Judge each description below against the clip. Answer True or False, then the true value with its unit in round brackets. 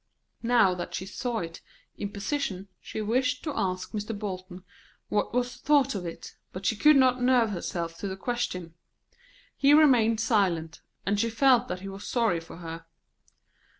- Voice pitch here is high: True (210 Hz)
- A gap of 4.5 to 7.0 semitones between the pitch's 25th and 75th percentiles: True (5.2 semitones)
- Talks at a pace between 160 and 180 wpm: True (170 wpm)